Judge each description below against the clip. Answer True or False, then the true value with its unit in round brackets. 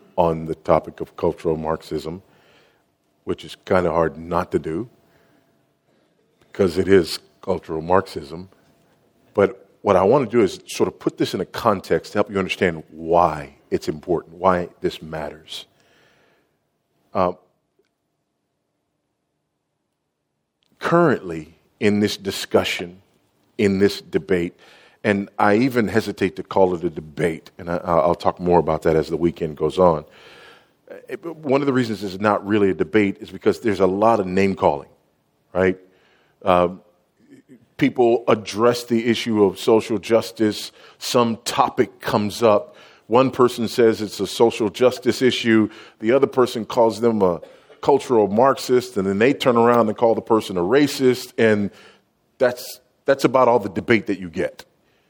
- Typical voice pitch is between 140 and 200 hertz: False (100 Hz)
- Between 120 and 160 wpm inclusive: True (150 wpm)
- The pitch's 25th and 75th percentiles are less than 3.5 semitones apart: False (4.3 semitones)